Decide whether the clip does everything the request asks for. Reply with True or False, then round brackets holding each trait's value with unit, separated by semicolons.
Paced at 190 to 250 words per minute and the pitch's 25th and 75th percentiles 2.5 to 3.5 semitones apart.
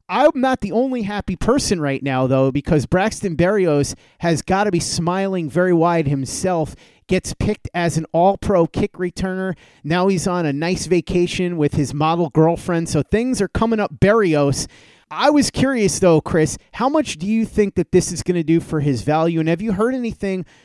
False (200 wpm; 4.0 semitones)